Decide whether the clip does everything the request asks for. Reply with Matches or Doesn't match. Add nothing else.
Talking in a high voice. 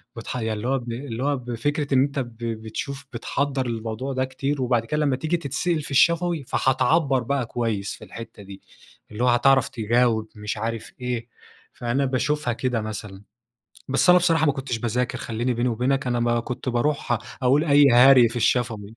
Doesn't match